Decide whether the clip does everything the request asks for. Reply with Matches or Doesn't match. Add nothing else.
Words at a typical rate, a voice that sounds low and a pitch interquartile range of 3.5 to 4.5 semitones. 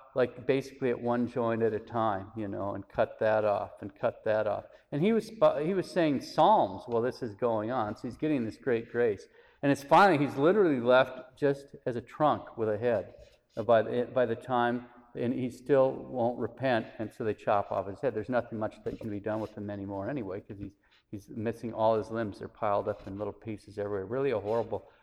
Doesn't match